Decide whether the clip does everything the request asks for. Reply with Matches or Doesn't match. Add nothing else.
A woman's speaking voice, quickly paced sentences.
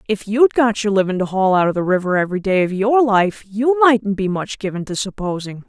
Matches